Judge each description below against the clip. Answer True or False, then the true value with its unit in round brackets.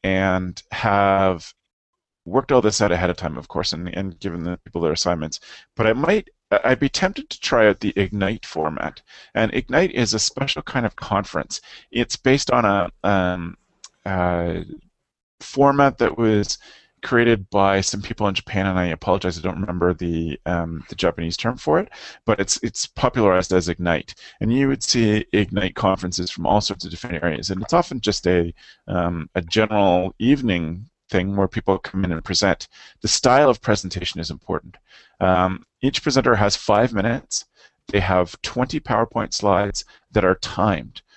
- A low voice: True (95 Hz)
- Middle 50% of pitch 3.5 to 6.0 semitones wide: True (4.1 semitones)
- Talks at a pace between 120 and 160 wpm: False (175 wpm)